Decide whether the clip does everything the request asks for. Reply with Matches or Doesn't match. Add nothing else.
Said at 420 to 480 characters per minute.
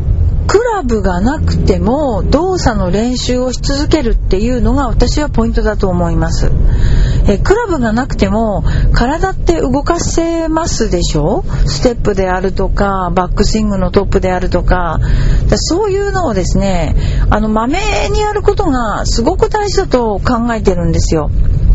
Doesn't match